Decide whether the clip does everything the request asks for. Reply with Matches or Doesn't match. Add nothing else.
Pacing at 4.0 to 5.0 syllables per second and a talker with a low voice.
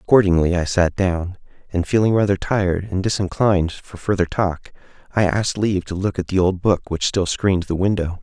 Doesn't match